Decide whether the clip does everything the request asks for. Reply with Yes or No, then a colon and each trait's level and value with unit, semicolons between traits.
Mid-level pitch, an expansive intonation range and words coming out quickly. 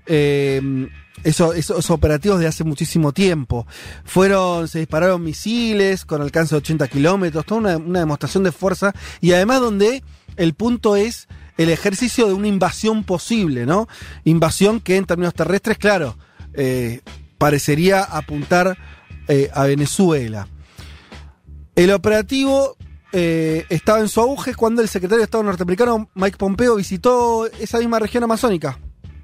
No: medium, 180 Hz; wide, 6.1 semitones; average, 140 wpm